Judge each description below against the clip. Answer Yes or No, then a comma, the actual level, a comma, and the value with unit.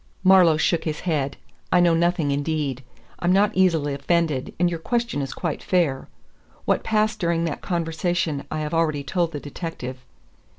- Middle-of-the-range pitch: Yes, medium, 165 Hz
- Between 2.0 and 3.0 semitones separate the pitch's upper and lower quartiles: No, average, 3.4 semitones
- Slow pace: No, average, 165 wpm